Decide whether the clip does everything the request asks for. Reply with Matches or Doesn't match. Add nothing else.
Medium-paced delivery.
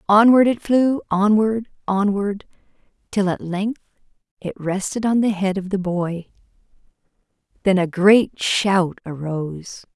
Doesn't match